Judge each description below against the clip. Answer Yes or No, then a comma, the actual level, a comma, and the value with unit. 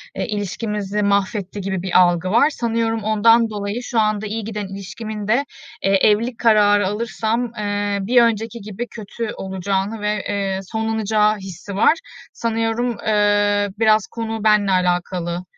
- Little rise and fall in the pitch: Yes, narrow, 2.1 semitones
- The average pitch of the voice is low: No, high, 210 Hz